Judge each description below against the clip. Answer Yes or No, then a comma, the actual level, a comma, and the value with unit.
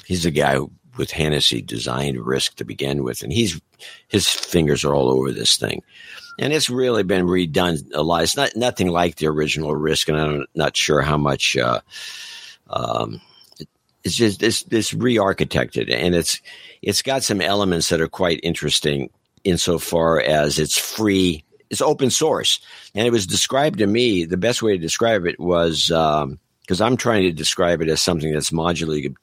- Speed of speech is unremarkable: Yes, average, 180 wpm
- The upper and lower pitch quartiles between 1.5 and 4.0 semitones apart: No, average, 4.6 semitones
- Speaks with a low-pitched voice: Yes, very low, 85 Hz